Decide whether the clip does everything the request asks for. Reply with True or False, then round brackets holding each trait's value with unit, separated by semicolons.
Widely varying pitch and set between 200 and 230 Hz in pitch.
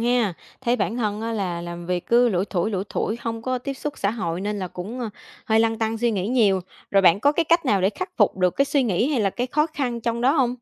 False (4.3 semitones; 225 Hz)